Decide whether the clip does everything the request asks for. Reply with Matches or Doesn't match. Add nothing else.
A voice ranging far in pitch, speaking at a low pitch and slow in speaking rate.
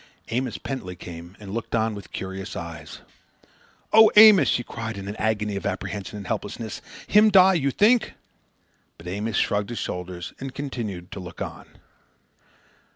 Doesn't match